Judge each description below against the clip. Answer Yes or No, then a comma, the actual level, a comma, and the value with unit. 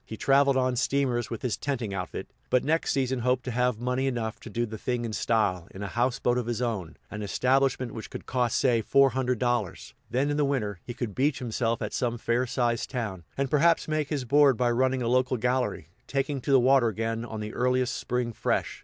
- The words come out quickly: Yes, fast, 225 wpm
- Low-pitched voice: Yes, low, 125 Hz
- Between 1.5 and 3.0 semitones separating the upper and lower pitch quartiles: Yes, narrow, 2.5 semitones